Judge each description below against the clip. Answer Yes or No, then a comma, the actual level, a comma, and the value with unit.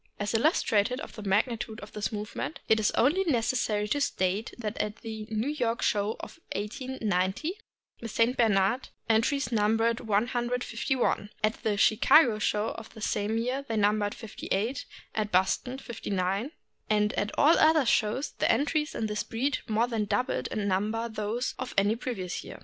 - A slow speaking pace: No, average, 170 wpm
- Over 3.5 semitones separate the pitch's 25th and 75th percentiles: No, average, 3.0 semitones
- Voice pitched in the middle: No, high, 225 Hz